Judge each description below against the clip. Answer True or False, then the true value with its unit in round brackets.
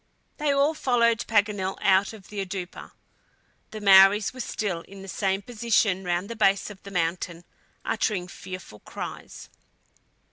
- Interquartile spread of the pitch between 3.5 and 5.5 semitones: False (2.7 semitones)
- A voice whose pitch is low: False (195 Hz)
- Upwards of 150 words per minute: False (145 wpm)